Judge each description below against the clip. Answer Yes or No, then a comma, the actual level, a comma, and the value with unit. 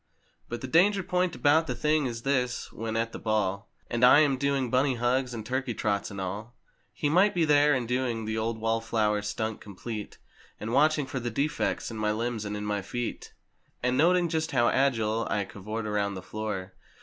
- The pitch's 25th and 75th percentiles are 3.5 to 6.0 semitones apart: Yes, average, 4.4 semitones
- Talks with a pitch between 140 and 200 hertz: No, low, 120 Hz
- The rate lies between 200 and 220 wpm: Yes, fast, 205 wpm